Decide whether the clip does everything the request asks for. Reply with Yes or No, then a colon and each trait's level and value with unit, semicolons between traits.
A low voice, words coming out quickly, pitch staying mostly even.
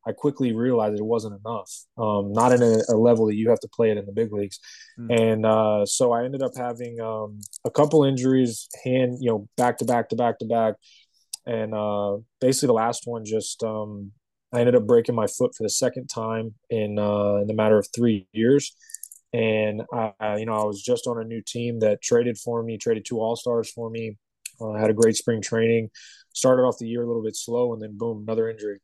Yes: low, 115 Hz; fast, 230 wpm; narrow, 1.9 semitones